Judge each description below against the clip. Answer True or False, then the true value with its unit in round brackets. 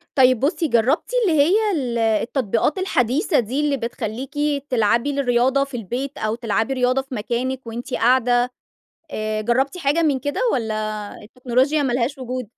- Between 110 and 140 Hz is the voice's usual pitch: False (250 Hz)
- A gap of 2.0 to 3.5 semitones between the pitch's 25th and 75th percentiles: True (3.0 semitones)